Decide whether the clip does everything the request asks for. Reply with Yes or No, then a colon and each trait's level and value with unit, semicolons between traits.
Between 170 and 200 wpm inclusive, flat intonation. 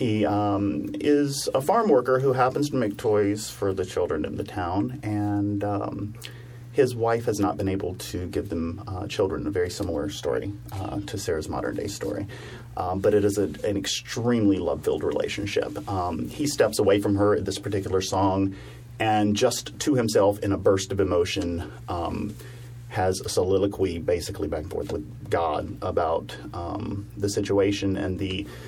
No: average, 180 wpm; average, 3.3 semitones